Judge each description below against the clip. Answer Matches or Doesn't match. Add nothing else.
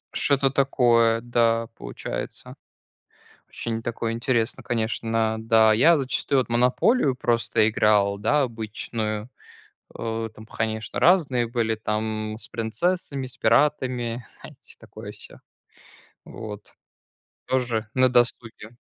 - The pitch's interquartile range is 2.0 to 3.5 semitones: Matches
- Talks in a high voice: Doesn't match